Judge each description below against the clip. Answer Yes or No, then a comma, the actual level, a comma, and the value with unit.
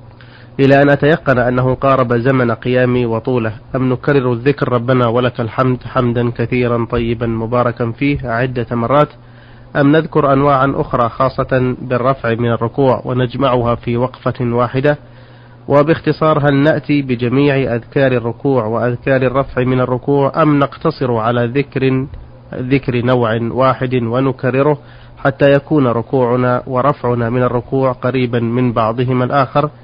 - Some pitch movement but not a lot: No, narrow, 2.3 semitones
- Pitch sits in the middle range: No, low, 125 Hz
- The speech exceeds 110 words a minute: Yes, average, 125 wpm